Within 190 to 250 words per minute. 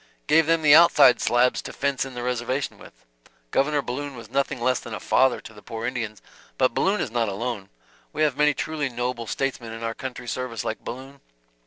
Yes: fast, 205 wpm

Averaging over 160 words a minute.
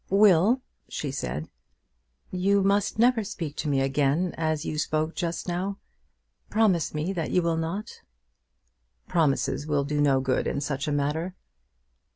No: average, 150 wpm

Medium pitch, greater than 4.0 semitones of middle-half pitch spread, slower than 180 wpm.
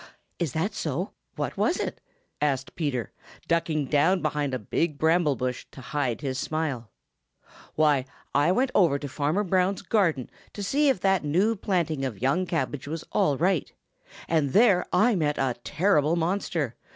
Yes: medium, 155 Hz; average, 4.6 semitones; average, 165 wpm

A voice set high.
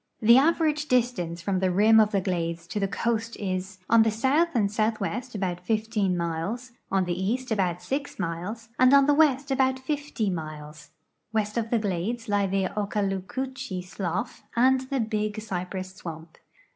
Yes: high, 210 Hz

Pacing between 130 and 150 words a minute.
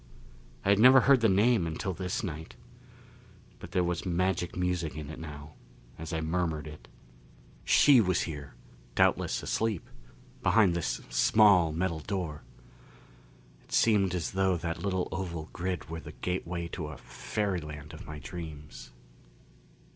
Yes: average, 145 wpm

